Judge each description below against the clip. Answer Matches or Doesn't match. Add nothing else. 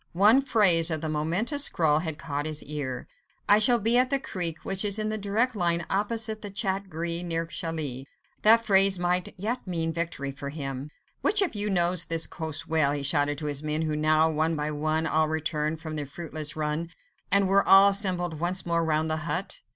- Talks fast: Matches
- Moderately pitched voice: Matches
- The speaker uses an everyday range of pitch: Matches